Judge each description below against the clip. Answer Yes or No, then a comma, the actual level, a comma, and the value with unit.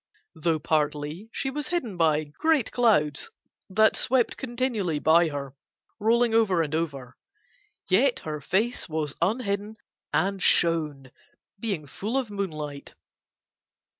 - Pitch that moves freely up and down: Yes, wide, 6.9 semitones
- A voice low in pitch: No, medium, 185 Hz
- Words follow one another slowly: Yes, slow, 120 wpm